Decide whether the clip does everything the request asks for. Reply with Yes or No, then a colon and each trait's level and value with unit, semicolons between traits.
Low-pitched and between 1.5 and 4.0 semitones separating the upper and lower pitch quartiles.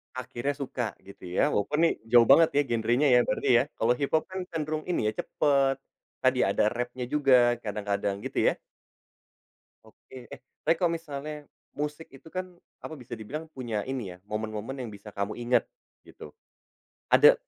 No: low, 130 Hz; average, 5.3 semitones